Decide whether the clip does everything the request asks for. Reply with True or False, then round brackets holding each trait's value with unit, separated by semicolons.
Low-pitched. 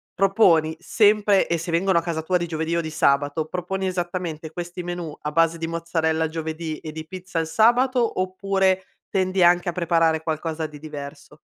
False (170 Hz)